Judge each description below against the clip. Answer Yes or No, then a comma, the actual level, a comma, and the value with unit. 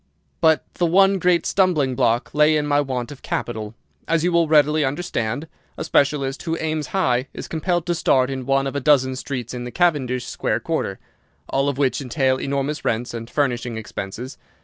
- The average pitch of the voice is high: No, medium, 140 Hz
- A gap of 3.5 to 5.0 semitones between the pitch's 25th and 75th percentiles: Yes, average, 3.9 semitones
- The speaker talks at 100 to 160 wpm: No, average, 190 wpm